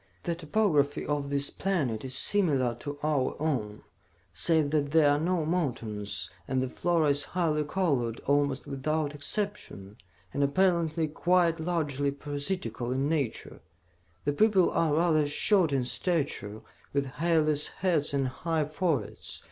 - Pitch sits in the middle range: Yes, medium, 145 Hz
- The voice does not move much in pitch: No, average, 3.4 semitones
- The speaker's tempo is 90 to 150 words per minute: Yes, average, 140 wpm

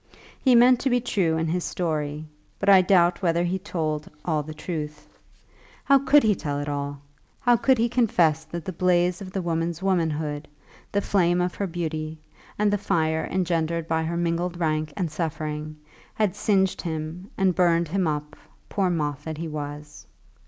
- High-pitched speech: No, medium, 170 Hz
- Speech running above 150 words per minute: Yes, average, 180 wpm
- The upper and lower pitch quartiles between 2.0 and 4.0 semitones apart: Yes, average, 3.3 semitones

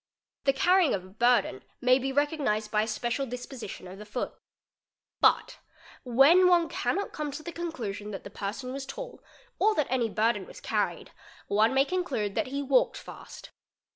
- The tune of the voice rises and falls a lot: Yes, wide, 5.7 semitones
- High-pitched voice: Yes, very high, 255 Hz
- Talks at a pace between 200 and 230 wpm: No, average, 175 wpm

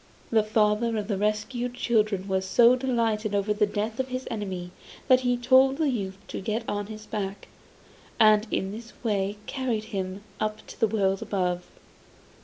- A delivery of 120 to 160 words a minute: No, average, 180 wpm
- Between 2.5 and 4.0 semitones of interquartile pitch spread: Yes, average, 2.8 semitones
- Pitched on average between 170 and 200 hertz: No, high, 215 Hz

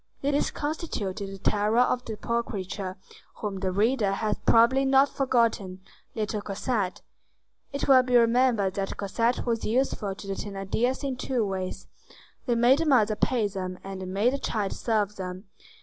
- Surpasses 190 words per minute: No, average, 165 wpm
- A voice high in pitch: Yes, high, 215 Hz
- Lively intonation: No, average, 4.3 semitones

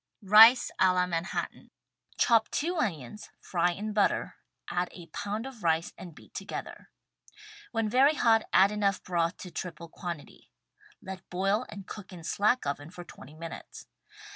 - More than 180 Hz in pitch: Yes, high, 190 Hz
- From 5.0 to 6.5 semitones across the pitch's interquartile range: No, average, 4.1 semitones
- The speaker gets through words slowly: No, average, 165 wpm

